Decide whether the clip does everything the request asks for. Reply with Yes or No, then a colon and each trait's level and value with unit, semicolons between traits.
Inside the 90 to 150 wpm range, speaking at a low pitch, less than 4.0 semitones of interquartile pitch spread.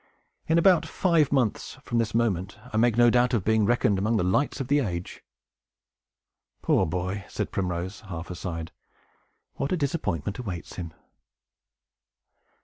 No: average, 145 wpm; low, 110 Hz; wide, 5.5 semitones